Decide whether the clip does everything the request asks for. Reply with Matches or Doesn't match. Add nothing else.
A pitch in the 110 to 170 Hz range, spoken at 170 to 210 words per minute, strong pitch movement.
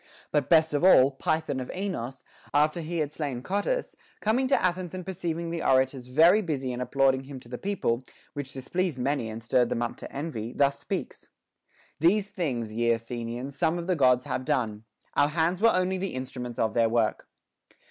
Matches